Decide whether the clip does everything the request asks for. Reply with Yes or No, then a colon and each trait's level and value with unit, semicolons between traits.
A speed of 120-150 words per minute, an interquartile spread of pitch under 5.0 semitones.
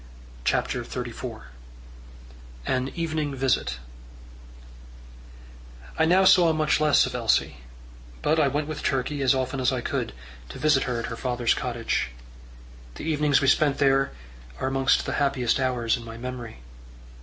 Yes: average, 145 wpm; average, 3.3 semitones